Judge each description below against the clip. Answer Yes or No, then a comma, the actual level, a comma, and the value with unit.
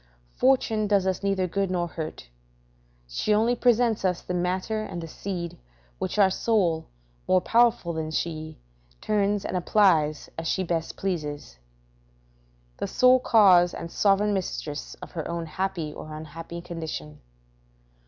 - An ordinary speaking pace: Yes, average, 145 wpm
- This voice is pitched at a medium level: Yes, medium, 180 Hz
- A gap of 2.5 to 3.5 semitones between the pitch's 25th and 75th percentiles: No, average, 3.9 semitones